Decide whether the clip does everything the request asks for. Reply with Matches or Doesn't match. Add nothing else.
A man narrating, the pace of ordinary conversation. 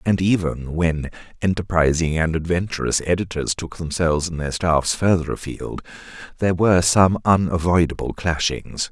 Doesn't match